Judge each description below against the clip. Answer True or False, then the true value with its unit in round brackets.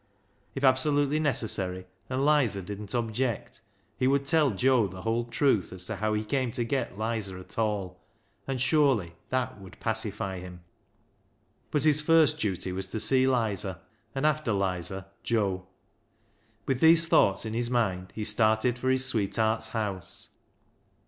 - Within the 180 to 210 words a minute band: False (155 wpm)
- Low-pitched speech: True (115 Hz)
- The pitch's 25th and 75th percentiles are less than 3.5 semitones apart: False (5.1 semitones)